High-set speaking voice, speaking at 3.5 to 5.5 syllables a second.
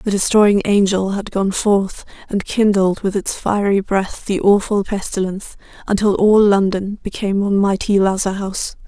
Yes: high, 200 Hz; 4.9 syllables/s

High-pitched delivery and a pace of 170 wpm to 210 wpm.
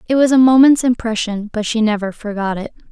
Yes: high, 230 Hz; fast, 205 wpm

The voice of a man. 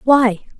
No: female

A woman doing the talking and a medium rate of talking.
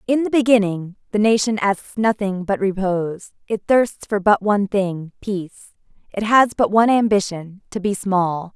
Yes: female; average, 170 wpm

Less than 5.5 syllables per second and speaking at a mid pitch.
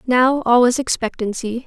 No: 4.7 syllables/s; high, 245 Hz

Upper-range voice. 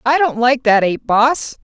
Yes: high, 245 Hz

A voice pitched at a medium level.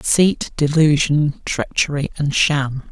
Yes: medium, 145 Hz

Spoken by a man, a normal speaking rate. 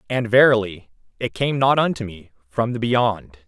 Yes: male; average, 175 wpm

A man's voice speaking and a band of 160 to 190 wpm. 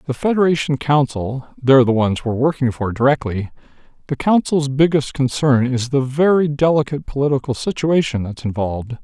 No: male; slow, 135 wpm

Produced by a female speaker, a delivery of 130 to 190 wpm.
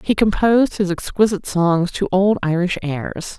Yes: female; average, 160 wpm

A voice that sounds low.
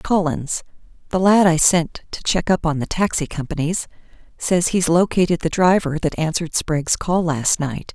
No: medium, 165 Hz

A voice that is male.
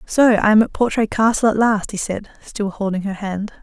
No: female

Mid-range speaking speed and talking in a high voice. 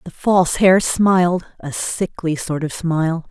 No: average, 165 wpm; medium, 175 Hz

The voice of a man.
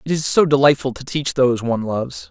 Yes: male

